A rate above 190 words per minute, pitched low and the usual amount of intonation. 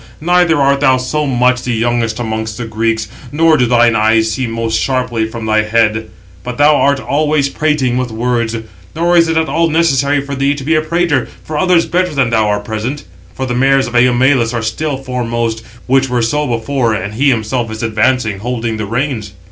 Yes: fast, 205 wpm; low, 125 Hz; average, 4.0 semitones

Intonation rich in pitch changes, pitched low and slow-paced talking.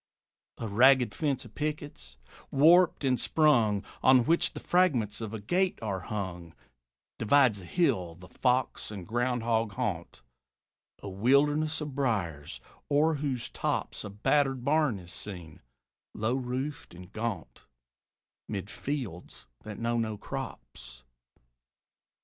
Yes: wide, 6.1 semitones; low, 120 Hz; slow, 130 wpm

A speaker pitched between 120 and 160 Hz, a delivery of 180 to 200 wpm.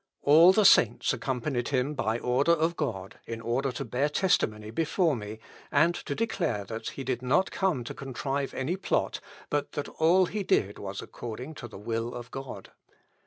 Yes: low, 135 Hz; average, 185 wpm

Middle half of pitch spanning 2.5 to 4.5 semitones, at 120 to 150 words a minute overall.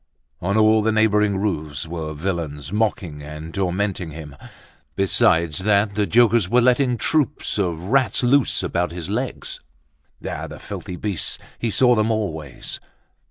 No: average, 5.1 semitones; average, 145 wpm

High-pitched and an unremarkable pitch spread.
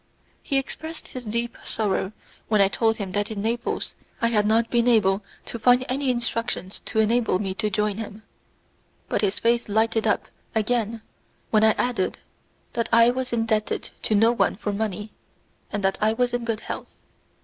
No: high, 225 Hz; narrow, 2.2 semitones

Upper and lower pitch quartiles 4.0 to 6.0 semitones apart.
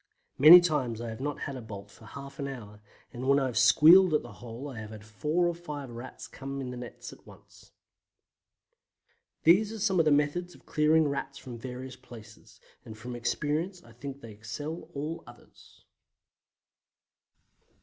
Yes: average, 4.6 semitones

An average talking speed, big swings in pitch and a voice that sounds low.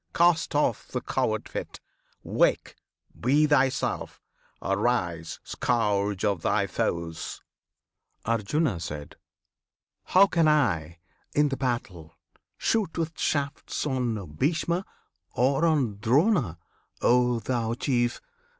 No: slow, 100 wpm; wide, 6.6 semitones; low, 125 Hz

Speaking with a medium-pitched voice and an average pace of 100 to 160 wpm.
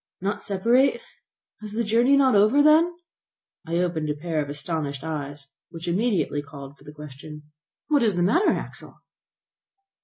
Yes: medium, 175 Hz; average, 155 wpm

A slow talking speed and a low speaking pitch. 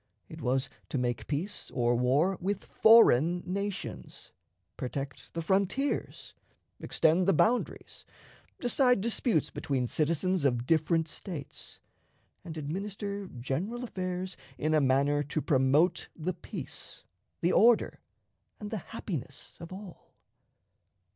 No: slow, 115 wpm; medium, 170 Hz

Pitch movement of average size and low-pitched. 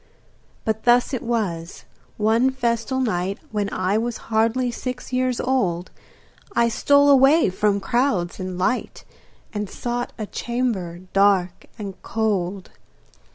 No: average, 4.3 semitones; high, 220 Hz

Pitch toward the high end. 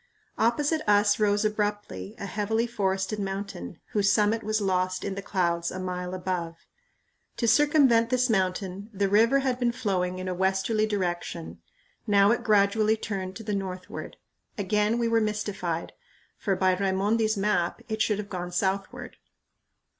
Yes: high, 205 Hz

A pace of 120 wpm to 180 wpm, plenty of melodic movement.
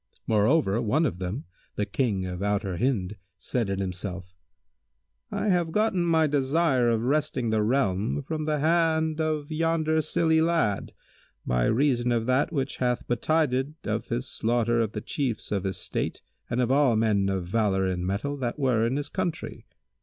Yes: average, 170 wpm; wide, 6.9 semitones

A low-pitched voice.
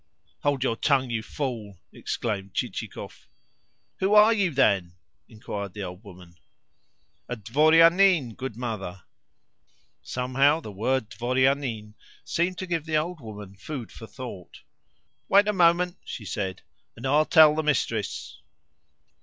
Yes: low, 130 Hz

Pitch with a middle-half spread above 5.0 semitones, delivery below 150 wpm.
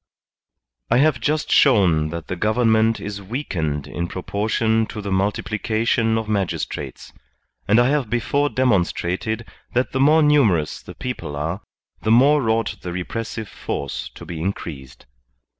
Yes: wide, 5.4 semitones; average, 140 wpm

